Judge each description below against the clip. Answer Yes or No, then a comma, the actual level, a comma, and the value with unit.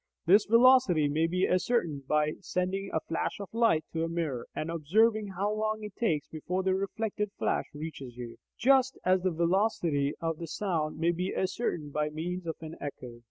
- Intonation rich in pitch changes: No, average, 4.9 semitones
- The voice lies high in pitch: No, medium, 175 Hz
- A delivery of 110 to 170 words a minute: No, average, 180 wpm